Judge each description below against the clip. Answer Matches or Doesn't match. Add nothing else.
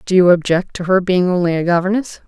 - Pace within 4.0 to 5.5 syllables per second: Doesn't match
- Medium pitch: Matches